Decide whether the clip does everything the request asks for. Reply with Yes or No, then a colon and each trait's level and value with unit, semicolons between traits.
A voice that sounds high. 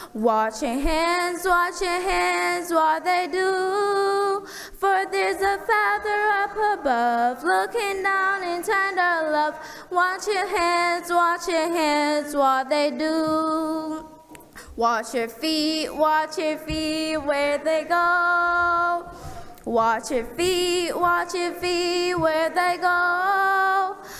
Yes: very high, 345 Hz